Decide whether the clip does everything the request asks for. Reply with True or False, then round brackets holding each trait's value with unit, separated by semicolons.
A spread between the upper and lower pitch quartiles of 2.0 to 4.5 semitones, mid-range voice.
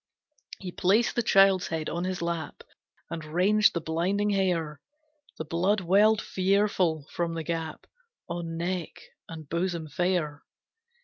True (2.9 semitones; 175 Hz)